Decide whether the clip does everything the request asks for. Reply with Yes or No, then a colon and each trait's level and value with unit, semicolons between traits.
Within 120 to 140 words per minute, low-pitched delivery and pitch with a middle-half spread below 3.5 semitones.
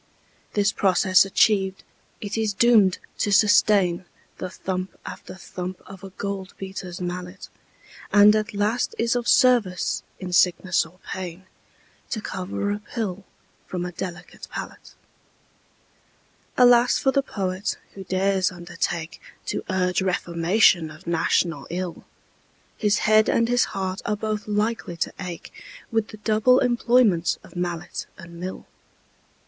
No: slow, 135 wpm; high, 190 Hz; average, 2.9 semitones